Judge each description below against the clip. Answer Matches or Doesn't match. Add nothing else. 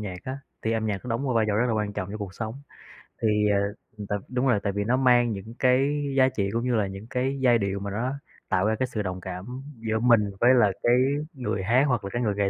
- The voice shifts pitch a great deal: Doesn't match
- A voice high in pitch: Doesn't match